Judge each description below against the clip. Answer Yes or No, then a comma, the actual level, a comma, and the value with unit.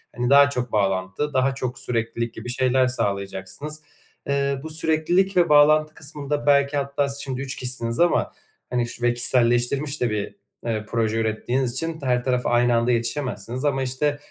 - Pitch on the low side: Yes, low, 130 Hz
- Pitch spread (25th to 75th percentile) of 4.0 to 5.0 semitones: No, average, 3.5 semitones